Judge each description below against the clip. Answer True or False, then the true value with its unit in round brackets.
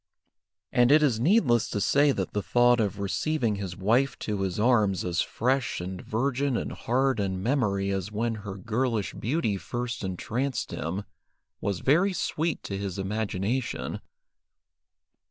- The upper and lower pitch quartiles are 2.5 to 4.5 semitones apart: False (4.9 semitones)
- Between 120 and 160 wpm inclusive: True (150 wpm)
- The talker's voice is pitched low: True (110 Hz)